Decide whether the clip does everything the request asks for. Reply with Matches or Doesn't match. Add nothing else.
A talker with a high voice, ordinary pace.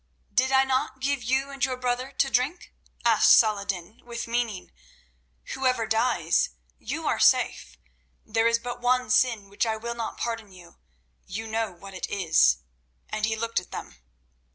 Matches